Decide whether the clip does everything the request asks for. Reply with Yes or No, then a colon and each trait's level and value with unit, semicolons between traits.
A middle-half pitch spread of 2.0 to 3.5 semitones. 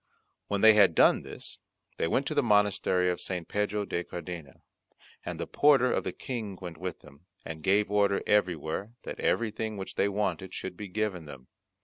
Yes: average, 3.2 semitones